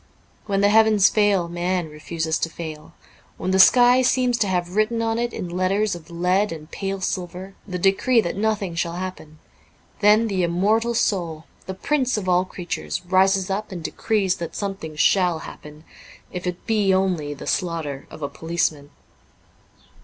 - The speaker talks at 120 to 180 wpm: Yes, average, 170 wpm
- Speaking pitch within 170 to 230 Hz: Yes, medium, 185 Hz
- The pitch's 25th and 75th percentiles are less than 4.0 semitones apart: Yes, average, 3.5 semitones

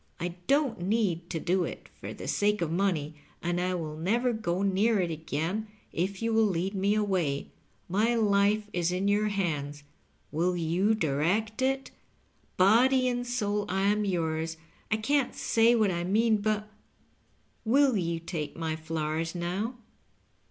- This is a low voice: No, high, 195 Hz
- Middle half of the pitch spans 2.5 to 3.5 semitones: No, average, 4.4 semitones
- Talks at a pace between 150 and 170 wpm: Yes, average, 165 wpm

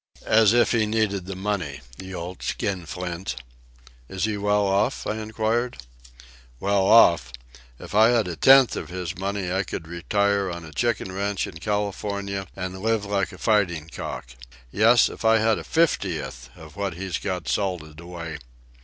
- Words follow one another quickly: No, average, 160 wpm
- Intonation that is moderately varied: Yes, average, 3.3 semitones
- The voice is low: Yes, very low, 95 Hz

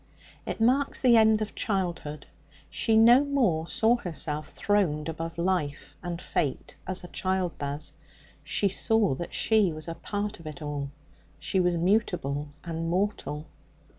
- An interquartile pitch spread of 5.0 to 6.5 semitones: Yes, wide, 5.4 semitones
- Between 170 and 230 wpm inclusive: No, average, 150 wpm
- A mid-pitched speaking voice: Yes, medium, 180 Hz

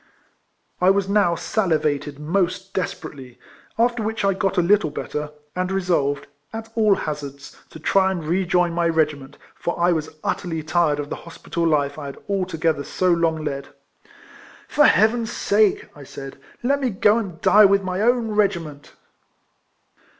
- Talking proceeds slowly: No, average, 165 wpm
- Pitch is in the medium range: Yes, medium, 175 Hz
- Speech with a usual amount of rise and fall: Yes, average, 4.6 semitones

